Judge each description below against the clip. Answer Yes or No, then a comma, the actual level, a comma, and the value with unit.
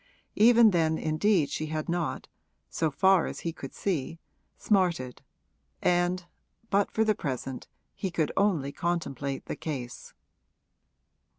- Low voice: No, medium, 170 Hz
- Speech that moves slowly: Yes, slow, 125 wpm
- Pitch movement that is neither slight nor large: Yes, average, 4.7 semitones